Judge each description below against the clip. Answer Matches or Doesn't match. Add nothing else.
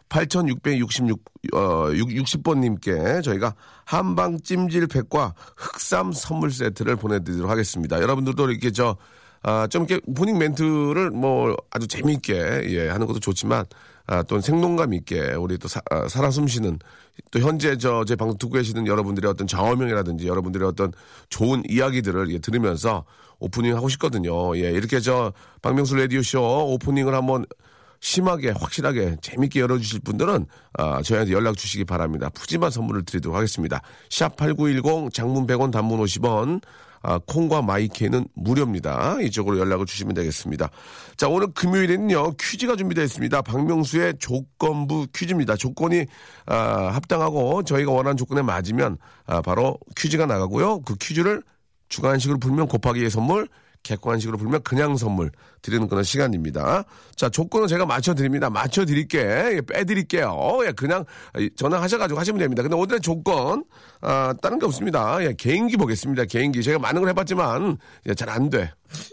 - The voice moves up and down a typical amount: Doesn't match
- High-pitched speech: Doesn't match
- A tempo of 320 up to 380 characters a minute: Matches